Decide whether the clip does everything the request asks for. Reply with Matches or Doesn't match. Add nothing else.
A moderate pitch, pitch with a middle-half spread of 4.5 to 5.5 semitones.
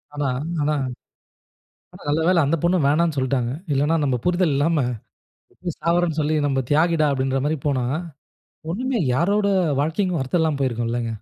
Doesn't match